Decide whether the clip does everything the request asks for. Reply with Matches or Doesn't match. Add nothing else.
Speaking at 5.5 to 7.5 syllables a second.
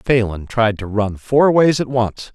Doesn't match